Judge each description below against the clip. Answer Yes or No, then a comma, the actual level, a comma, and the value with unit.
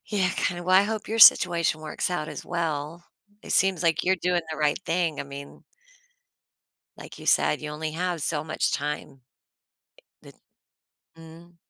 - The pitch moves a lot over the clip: No, average, 2.8 semitones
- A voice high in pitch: No, medium, 170 Hz